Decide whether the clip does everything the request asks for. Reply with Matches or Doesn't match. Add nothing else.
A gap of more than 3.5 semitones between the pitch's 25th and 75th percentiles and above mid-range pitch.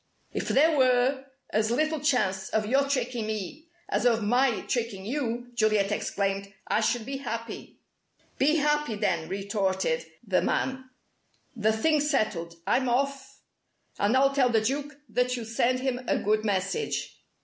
Matches